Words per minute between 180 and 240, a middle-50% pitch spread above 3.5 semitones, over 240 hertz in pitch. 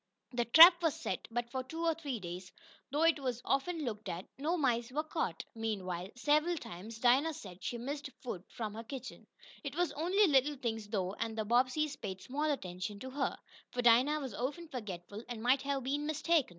Yes: average, 200 wpm; average, 5.2 semitones; very high, 255 Hz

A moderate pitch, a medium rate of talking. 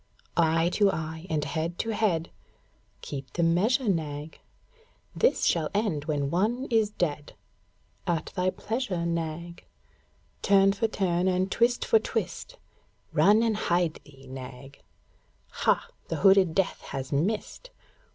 No: medium, 175 Hz; slow, 130 wpm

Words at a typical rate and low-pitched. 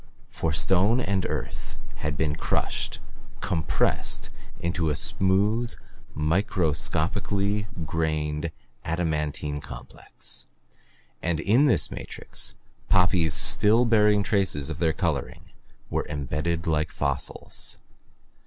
No: slow, 95 wpm; very low, 85 Hz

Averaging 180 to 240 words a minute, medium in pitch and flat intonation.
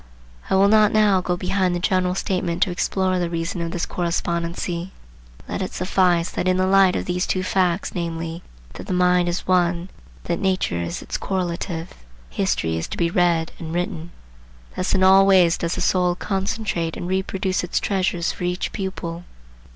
Yes: average, 185 wpm; medium, 180 Hz; narrow, 1.8 semitones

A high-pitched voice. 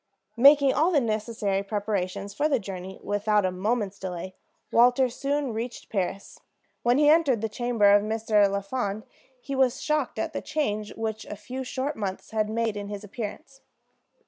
Yes: high, 220 Hz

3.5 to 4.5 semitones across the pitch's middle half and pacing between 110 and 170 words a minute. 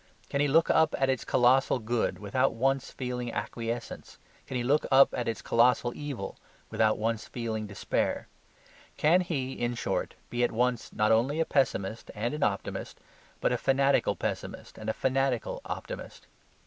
No: average, 3.0 semitones; average, 165 wpm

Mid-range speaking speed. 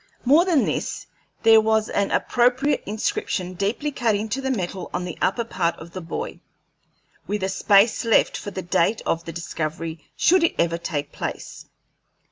Yes: average, 170 wpm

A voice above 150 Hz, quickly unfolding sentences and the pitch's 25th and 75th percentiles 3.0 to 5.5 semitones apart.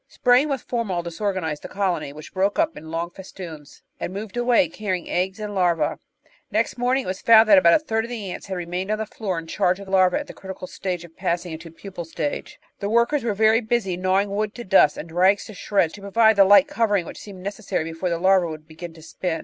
Yes: high, 190 Hz; fast, 240 wpm; average, 4.0 semitones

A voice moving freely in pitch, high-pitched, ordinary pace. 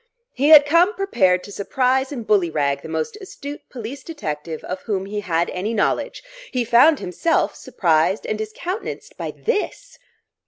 Yes: wide, 8.3 semitones; high, 225 Hz; average, 160 wpm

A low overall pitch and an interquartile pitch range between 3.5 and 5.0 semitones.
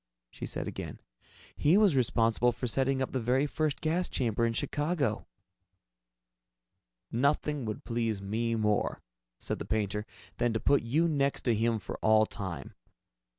Yes: low, 120 Hz; average, 4.2 semitones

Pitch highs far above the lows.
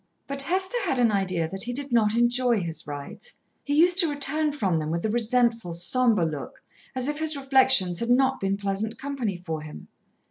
Yes: wide, 6.9 semitones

